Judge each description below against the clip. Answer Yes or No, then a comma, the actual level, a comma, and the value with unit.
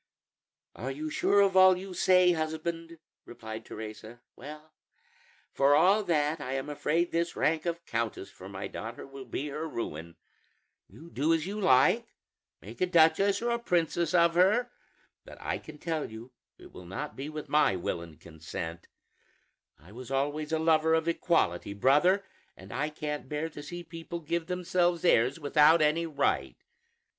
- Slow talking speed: No, average, 170 wpm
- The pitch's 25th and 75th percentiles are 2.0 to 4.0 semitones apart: No, average, 4.7 semitones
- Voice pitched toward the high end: No, medium, 155 Hz